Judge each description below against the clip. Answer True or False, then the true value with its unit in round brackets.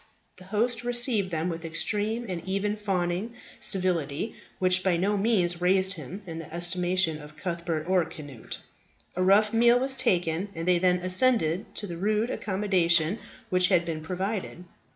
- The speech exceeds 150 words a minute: True (160 wpm)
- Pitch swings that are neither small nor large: True (3.4 semitones)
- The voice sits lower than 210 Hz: True (185 Hz)